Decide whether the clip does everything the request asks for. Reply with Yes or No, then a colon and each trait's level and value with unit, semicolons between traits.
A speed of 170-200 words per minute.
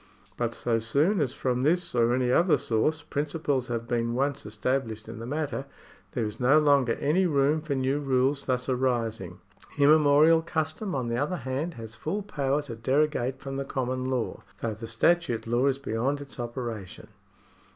Yes: average, 175 wpm